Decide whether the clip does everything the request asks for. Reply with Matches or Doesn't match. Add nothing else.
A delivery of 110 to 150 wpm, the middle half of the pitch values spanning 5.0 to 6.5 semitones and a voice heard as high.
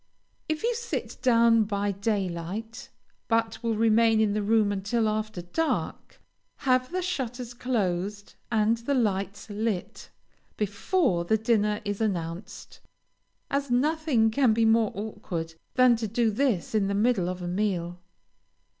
Doesn't match